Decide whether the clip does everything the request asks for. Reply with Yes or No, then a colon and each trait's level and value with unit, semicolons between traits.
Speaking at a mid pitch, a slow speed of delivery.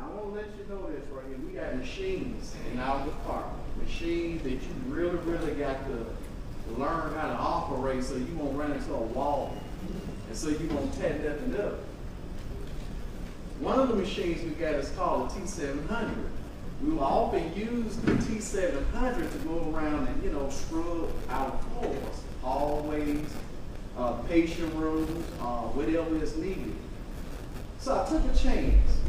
No: medium, 160 Hz; average, 170 wpm